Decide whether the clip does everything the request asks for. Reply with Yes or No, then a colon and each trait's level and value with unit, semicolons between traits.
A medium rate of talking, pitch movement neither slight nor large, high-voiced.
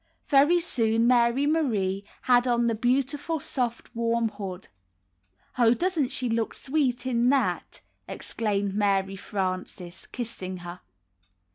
No: slow, 120 wpm; average, 4.6 semitones; high, 235 Hz